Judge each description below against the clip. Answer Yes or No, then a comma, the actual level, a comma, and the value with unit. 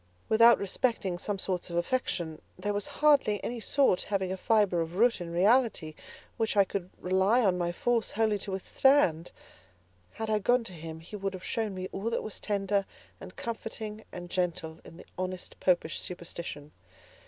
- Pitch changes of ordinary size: Yes, average, 3.9 semitones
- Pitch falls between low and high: No, high, 195 Hz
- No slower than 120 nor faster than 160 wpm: No, average, 175 wpm